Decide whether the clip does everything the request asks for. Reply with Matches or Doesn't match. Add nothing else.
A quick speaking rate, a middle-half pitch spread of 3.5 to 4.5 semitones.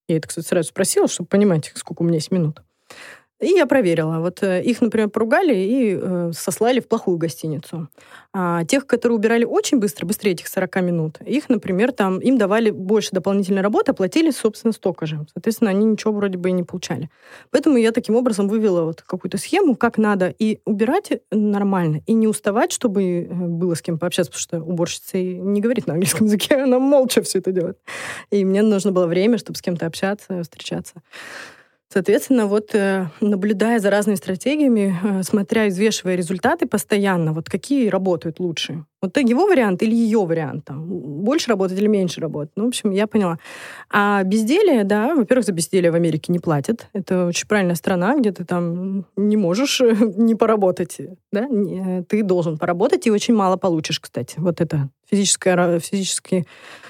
Matches